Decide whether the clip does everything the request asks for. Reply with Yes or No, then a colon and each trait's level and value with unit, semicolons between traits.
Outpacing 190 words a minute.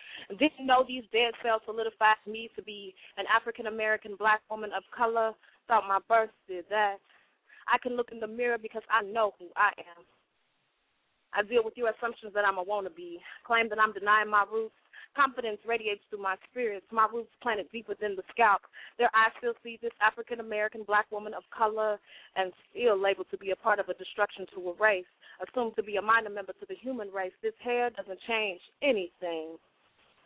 Yes: average, 200 wpm